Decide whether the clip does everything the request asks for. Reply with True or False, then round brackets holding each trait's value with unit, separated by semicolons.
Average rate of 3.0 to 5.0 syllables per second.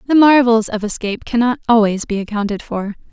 False (5.9 syllables/s)